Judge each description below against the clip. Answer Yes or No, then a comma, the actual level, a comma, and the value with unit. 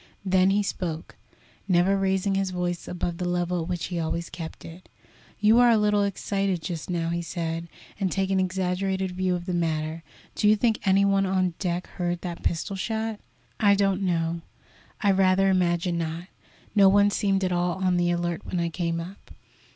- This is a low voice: No, medium, 185 Hz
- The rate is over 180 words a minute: Yes, average, 190 wpm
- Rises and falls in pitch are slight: Yes, narrow, 2.1 semitones